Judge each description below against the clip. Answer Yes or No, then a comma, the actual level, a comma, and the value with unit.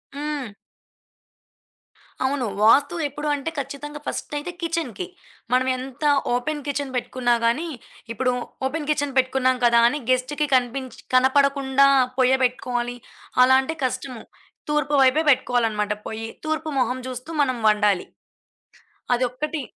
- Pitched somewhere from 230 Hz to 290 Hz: Yes, very high, 260 Hz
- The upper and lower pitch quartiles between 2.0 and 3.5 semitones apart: Yes, average, 2.9 semitones